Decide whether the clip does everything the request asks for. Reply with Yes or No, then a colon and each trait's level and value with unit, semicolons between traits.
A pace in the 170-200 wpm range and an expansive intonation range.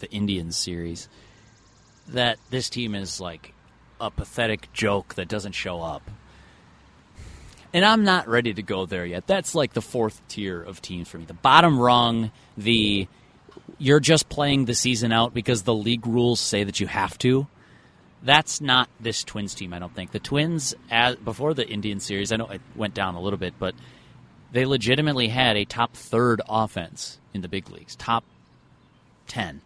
No: average, 175 wpm; average, 4.2 semitones